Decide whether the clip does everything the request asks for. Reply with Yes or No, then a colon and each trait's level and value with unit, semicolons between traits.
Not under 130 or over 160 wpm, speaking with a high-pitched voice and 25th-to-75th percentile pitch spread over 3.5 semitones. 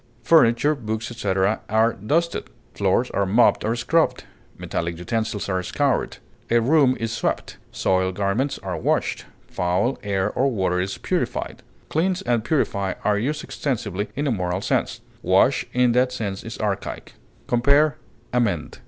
No: average, 145 wpm; low, 115 Hz; average, 4.8 semitones